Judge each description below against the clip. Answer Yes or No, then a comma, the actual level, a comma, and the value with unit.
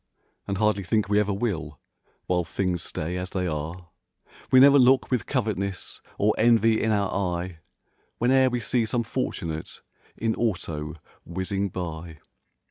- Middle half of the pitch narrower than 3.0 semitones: No, average, 4.5 semitones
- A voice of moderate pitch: No, low, 100 Hz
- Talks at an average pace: Yes, average, 145 wpm